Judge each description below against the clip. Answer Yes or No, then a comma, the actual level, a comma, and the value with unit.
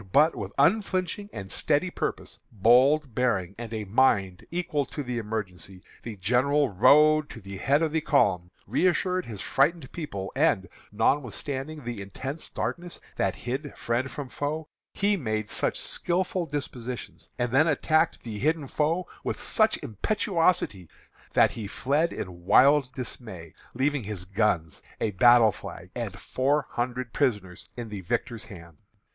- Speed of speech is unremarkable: Yes, average, 145 wpm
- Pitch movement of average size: No, wide, 6.5 semitones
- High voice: No, low, 125 Hz